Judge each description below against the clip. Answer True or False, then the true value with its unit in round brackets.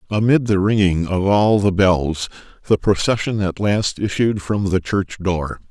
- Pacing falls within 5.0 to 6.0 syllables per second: False (4.2 syllables/s)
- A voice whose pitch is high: False (100 Hz)